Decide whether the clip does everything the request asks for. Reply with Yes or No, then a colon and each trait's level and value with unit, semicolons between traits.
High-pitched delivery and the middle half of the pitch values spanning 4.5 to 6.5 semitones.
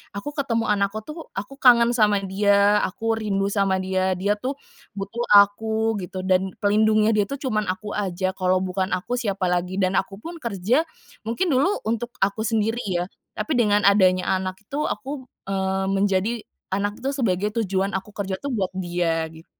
No: high, 205 Hz; average, 3.2 semitones